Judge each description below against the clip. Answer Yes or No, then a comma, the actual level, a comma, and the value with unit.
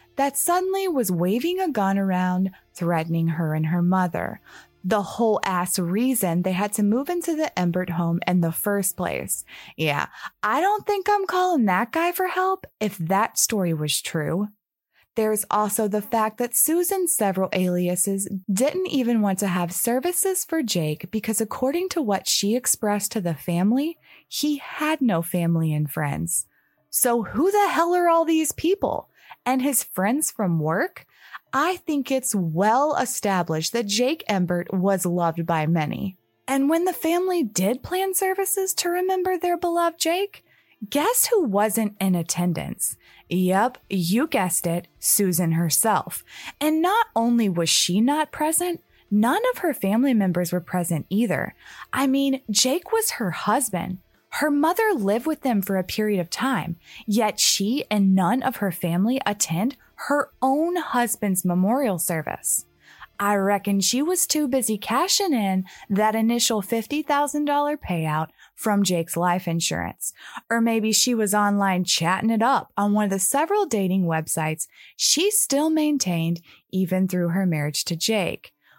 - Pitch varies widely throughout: Yes, wide, 8.2 semitones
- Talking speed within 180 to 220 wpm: No, average, 155 wpm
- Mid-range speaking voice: No, high, 215 Hz